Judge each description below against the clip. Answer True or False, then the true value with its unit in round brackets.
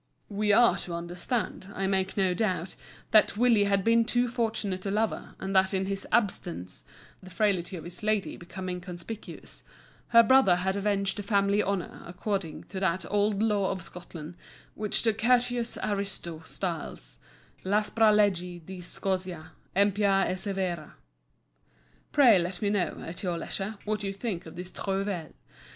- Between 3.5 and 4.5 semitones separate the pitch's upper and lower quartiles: False (2.8 semitones)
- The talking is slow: False (155 wpm)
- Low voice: False (195 Hz)